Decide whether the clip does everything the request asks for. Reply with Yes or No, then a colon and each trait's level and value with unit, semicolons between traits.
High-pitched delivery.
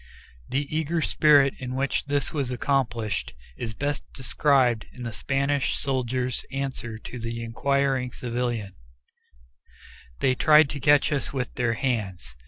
No: low, 130 Hz